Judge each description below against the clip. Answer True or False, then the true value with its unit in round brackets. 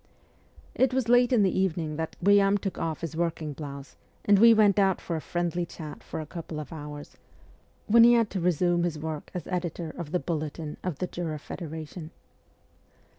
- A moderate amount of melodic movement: True (3.8 semitones)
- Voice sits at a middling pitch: True (170 Hz)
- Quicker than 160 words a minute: True (205 wpm)